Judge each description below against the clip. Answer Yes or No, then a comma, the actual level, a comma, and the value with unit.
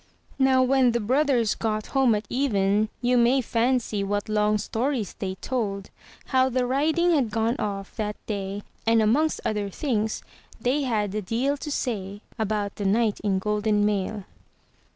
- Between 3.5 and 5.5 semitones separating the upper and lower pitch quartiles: Yes, average, 3.8 semitones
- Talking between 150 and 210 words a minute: Yes, average, 160 wpm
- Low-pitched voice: No, high, 220 Hz